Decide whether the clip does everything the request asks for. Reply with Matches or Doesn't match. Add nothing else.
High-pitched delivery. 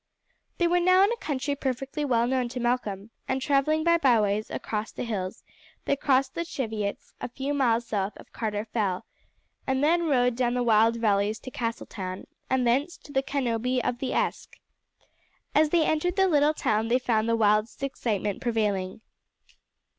Matches